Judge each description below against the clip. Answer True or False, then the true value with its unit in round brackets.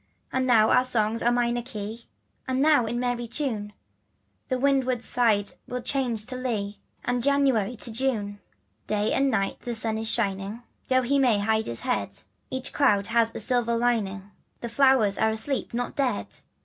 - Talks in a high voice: True (235 Hz)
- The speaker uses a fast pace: False (175 wpm)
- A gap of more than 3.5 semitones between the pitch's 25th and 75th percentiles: False (3.0 semitones)